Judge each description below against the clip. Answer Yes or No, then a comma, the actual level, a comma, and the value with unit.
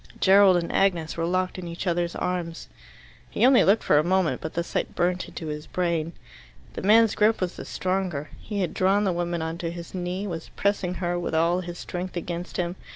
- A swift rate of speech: Yes, fast, 215 wpm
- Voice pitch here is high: No, medium, 175 Hz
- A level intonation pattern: Yes, narrow, 1.8 semitones